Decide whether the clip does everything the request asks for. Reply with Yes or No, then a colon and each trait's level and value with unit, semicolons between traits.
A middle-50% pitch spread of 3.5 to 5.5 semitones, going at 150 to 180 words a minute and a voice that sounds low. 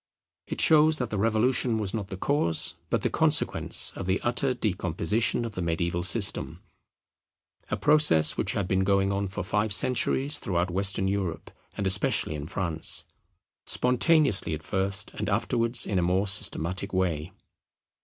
Yes: average, 4.2 semitones; average, 155 wpm; low, 100 Hz